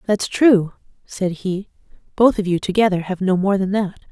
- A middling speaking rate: Yes, average, 190 wpm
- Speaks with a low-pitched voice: No, high, 195 Hz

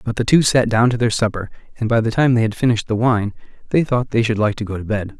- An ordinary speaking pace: No, fast, 300 wpm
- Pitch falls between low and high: No, low, 115 Hz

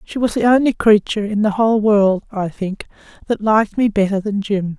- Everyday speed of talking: No, fast, 215 wpm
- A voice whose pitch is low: No, high, 210 Hz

